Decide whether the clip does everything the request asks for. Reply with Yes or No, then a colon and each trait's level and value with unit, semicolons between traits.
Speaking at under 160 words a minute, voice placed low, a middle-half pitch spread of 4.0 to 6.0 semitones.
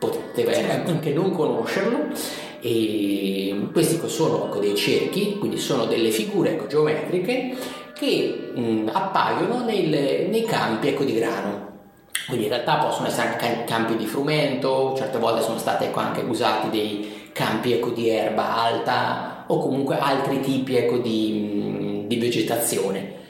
Yes: average, 120 wpm; low, 115 Hz; average, 4.3 semitones